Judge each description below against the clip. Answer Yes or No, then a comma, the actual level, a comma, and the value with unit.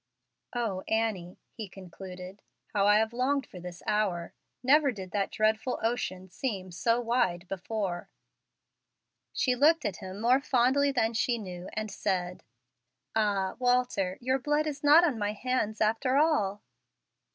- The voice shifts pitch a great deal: No, average, 4.9 semitones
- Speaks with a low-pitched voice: No, high, 220 Hz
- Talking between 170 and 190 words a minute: No, average, 145 wpm